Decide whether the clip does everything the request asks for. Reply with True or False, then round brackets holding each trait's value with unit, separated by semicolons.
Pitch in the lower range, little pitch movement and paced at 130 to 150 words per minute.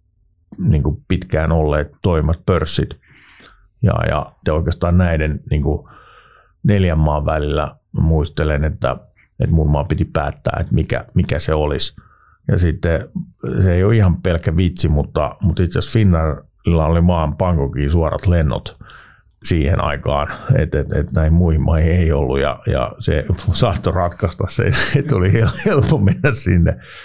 False (85 Hz; 3.2 semitones; 145 wpm)